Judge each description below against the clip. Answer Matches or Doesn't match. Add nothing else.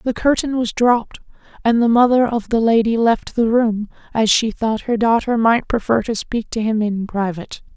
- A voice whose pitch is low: Doesn't match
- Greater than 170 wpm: Matches